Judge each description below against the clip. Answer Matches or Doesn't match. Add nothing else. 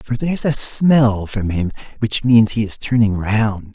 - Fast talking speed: Doesn't match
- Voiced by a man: Matches